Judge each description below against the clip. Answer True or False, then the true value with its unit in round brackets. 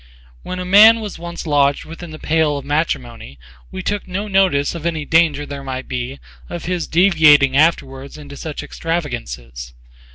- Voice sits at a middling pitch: True (155 Hz)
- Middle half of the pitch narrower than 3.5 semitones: False (3.8 semitones)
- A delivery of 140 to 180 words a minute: True (165 wpm)